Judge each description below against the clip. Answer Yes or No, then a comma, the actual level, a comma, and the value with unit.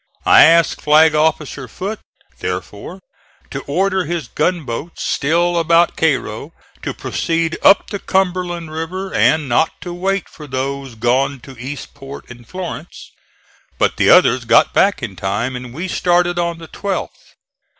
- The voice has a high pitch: No, medium, 160 Hz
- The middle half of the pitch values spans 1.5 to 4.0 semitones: No, average, 4.4 semitones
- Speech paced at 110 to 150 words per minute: Yes, average, 145 wpm